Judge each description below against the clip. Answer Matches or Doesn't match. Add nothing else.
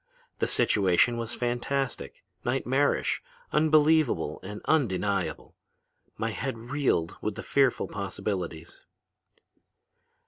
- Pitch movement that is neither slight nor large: Doesn't match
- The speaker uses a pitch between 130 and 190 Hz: Doesn't match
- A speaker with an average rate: Doesn't match